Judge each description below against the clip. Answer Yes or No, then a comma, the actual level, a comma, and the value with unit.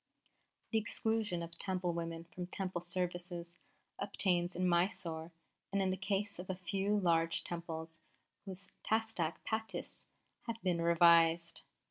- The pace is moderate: No, slow, 125 wpm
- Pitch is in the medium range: Yes, medium, 175 Hz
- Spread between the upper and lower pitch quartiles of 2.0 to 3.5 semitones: Yes, narrow, 2.4 semitones